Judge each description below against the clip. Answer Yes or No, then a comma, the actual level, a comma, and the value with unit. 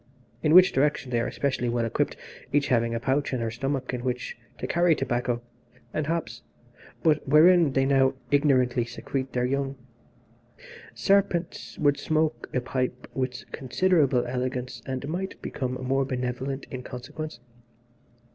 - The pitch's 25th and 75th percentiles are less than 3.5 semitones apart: Yes, average, 2.9 semitones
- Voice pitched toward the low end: Yes, low, 130 Hz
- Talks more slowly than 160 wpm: Yes, average, 145 wpm